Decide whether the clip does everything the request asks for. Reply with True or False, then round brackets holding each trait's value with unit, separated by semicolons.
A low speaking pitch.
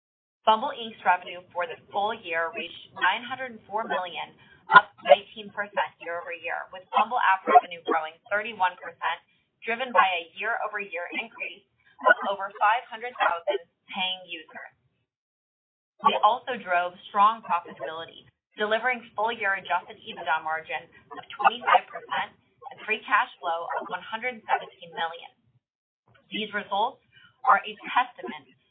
False (200 Hz)